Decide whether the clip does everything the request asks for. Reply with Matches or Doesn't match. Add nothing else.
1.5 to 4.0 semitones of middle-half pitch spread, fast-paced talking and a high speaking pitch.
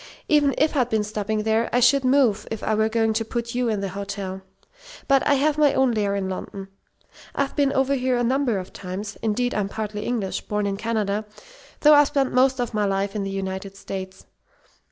Doesn't match